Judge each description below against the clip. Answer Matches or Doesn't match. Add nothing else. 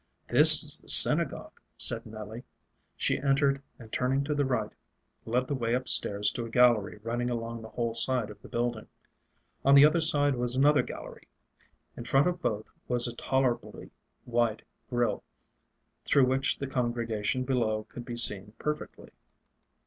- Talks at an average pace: Matches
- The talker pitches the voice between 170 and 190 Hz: Doesn't match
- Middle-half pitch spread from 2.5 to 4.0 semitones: Matches